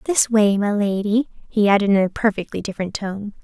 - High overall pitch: Yes, high, 205 Hz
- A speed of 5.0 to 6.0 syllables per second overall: Yes, 5.6 syllables/s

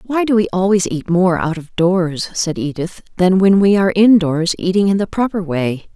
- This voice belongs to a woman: Yes, female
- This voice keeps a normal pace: No, fast, 210 wpm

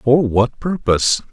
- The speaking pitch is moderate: No, low, 120 Hz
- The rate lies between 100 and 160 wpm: Yes, slow, 135 wpm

